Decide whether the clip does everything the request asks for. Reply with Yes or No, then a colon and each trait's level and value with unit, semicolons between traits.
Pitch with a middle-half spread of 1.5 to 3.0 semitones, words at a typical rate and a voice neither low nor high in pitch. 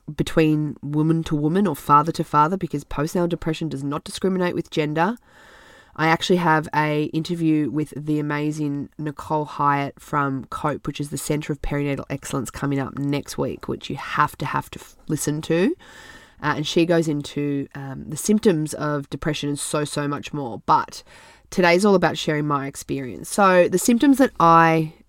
Yes: narrow, 2.5 semitones; average, 180 wpm; medium, 150 Hz